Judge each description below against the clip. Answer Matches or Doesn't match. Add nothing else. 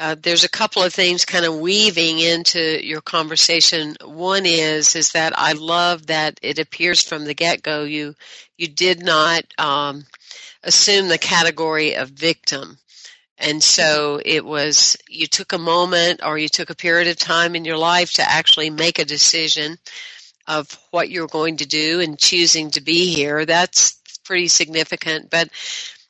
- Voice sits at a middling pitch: Matches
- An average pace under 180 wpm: Matches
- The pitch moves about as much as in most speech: Doesn't match